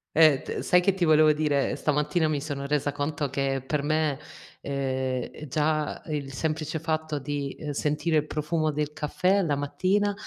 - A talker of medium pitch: Yes, medium, 150 Hz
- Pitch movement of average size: No, narrow, 1.7 semitones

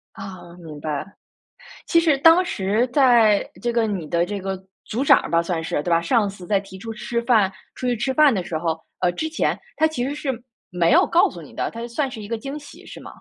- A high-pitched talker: Yes, high, 215 Hz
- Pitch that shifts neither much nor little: No, wide, 6.5 semitones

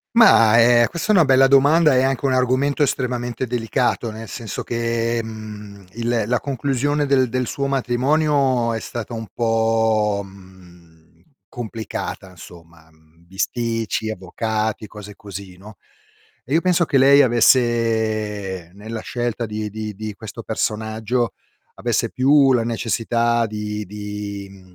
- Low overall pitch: Yes, low, 115 Hz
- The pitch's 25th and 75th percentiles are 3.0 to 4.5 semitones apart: Yes, average, 3.4 semitones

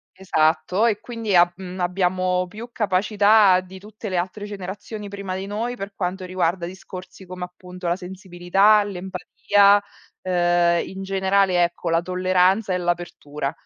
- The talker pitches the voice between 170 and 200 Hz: Yes, medium, 185 Hz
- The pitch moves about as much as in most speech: No, narrow, 2.1 semitones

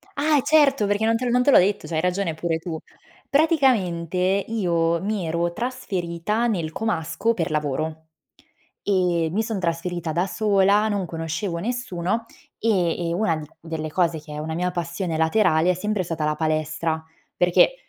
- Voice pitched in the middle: Yes, medium, 175 Hz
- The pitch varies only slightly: No, average, 4.6 semitones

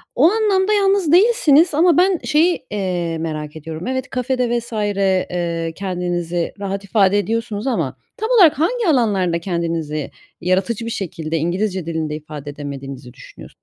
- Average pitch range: No, wide, 8.8 semitones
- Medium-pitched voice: No, high, 195 Hz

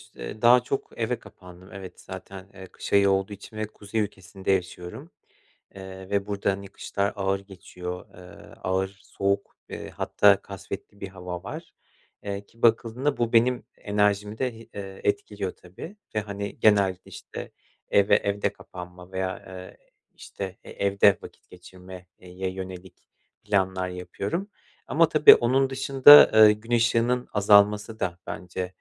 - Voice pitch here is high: No, low, 100 Hz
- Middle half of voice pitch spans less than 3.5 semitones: Yes, narrow, 2.5 semitones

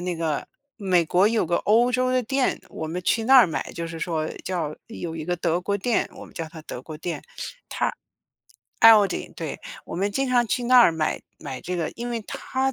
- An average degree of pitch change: No, wide, 6.2 semitones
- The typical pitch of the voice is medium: Yes, medium, 180 Hz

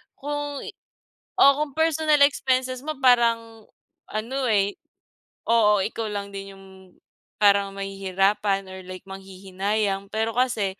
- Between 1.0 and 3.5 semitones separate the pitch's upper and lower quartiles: No, average, 4.6 semitones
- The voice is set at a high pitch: Yes, high, 210 Hz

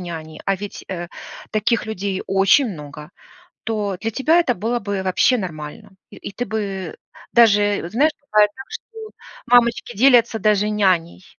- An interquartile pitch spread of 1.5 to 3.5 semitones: No, average, 3.9 semitones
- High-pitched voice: Yes, high, 210 Hz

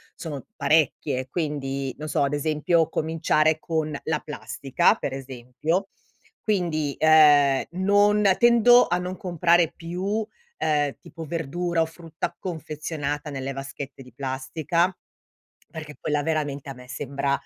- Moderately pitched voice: Yes, medium, 155 Hz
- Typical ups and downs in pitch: Yes, average, 3.3 semitones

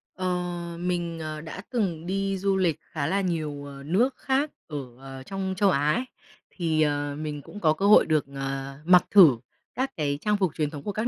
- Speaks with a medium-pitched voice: Yes, medium, 170 Hz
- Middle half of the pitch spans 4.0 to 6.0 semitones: Yes, average, 4.7 semitones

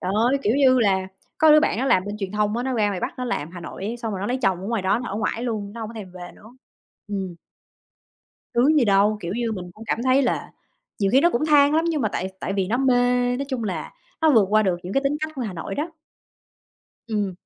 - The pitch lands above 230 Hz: No, high, 220 Hz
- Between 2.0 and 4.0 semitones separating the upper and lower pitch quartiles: No, average, 4.8 semitones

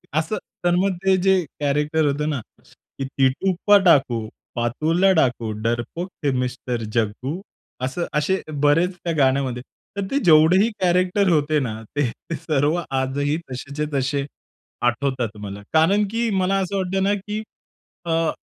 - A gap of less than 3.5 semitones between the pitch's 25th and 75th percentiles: No, wide, 5.6 semitones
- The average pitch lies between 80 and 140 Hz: No, medium, 150 Hz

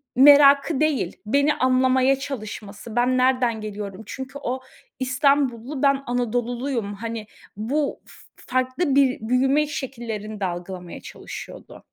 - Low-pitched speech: No, very high, 255 Hz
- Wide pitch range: No, average, 3.8 semitones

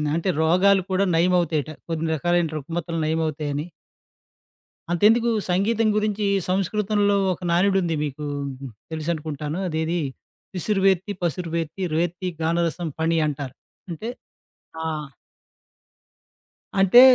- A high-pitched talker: No, medium, 170 Hz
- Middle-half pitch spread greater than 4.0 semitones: No, average, 3.3 semitones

